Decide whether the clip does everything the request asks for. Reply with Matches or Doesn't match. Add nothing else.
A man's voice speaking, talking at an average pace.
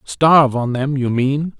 Matches